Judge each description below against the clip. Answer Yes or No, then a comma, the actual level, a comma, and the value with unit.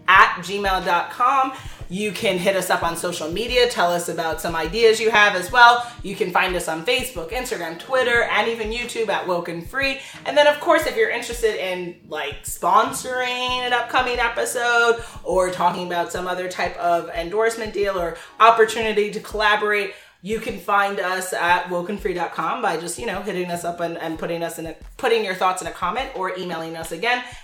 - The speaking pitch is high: Yes, high, 200 Hz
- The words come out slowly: No, average, 190 wpm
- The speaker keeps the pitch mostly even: No, average, 5.1 semitones